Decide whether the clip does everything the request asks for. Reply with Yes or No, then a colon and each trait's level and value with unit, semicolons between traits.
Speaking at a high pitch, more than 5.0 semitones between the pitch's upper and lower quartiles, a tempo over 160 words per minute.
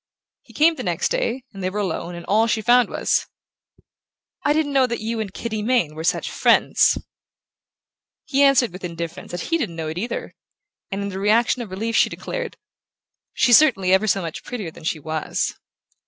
Yes: high, 215 Hz; wide, 5.6 semitones; average, 195 wpm